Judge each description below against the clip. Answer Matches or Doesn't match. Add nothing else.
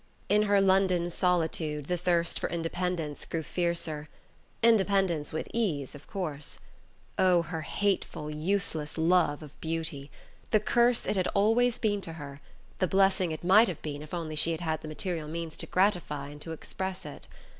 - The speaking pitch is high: Doesn't match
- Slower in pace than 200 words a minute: Matches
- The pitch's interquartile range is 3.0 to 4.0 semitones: Matches